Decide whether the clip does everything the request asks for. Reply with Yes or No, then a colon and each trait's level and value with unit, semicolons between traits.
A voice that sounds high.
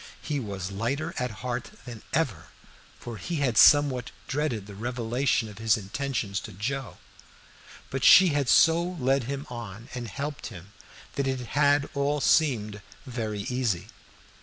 No: low, 125 Hz